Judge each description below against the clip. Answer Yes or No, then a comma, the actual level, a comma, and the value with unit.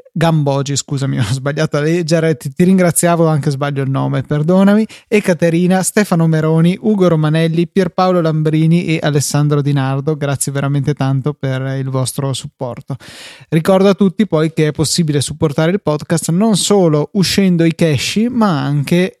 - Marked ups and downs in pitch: No, average, 3.8 semitones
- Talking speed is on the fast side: No, average, 155 wpm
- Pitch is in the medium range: Yes, medium, 160 Hz